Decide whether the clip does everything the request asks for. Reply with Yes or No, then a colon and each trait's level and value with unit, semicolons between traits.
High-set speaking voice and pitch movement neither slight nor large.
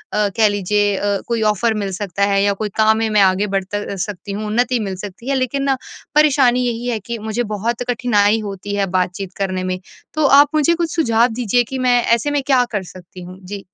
Yes: high, 215 Hz; average, 3.6 semitones